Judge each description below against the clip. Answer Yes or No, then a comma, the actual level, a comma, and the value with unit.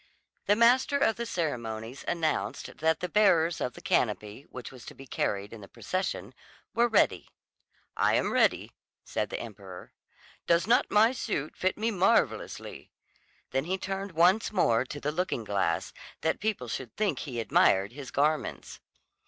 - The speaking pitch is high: No, medium, 160 Hz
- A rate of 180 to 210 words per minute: No, average, 160 wpm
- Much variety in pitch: Yes, wide, 8.9 semitones